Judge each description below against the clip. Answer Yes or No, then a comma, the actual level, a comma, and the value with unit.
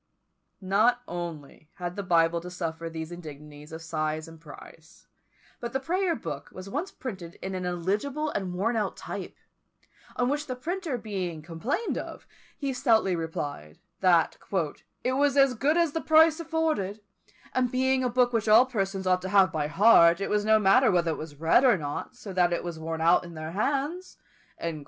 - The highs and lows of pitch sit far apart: Yes, wide, 7.4 semitones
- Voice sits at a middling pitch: No, high, 195 Hz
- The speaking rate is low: No, average, 185 wpm